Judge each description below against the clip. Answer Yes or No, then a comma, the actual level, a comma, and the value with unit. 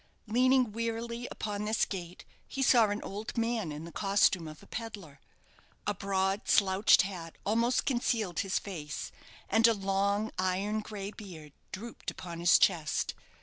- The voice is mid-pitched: No, high, 200 Hz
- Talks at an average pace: Yes, average, 150 wpm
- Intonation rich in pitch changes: No, average, 3.4 semitones